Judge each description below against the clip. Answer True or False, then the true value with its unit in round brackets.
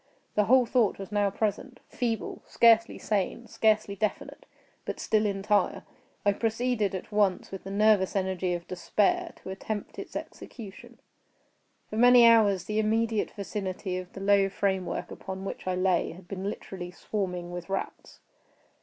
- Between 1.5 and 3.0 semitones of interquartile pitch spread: True (2.5 semitones)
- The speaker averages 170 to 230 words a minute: False (145 wpm)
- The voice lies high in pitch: True (200 Hz)